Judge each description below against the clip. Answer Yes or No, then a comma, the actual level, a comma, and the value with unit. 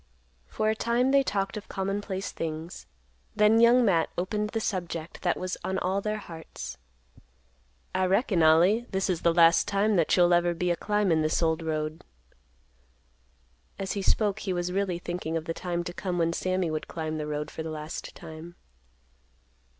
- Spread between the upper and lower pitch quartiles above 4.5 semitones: No, average, 3.4 semitones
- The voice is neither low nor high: Yes, medium, 180 Hz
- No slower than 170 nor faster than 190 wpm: Yes, average, 180 wpm